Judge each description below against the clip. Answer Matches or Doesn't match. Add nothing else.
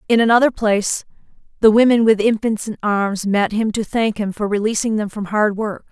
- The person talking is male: Doesn't match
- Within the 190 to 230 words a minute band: Matches